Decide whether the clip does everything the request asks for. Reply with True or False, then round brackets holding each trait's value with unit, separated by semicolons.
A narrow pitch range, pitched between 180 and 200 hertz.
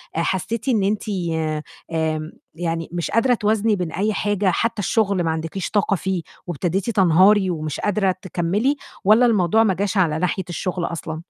False (3.9 semitones; 190 Hz)